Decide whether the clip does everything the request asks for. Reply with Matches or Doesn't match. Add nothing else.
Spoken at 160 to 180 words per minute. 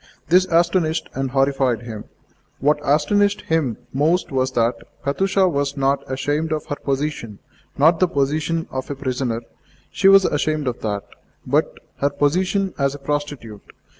Doesn't match